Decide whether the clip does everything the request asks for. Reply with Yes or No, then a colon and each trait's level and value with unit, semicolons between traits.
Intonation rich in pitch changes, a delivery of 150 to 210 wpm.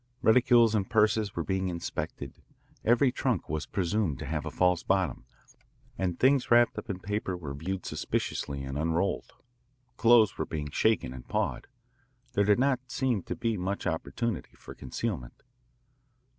Yes: wide, 5.9 semitones; average, 155 wpm